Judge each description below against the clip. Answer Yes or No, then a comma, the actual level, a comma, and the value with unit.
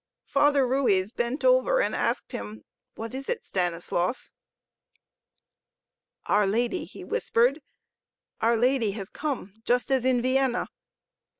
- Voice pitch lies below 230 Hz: No, high, 245 Hz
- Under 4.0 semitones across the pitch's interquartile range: No, average, 4.7 semitones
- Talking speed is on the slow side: Yes, slow, 120 wpm